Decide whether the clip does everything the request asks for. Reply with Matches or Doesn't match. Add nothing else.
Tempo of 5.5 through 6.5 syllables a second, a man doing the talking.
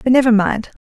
Doesn't match